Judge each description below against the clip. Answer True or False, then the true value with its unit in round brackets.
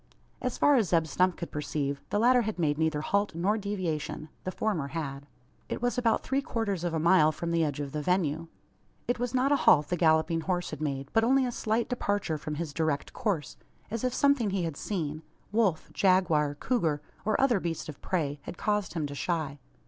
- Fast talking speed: True (210 wpm)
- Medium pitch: True (170 Hz)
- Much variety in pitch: True (5.9 semitones)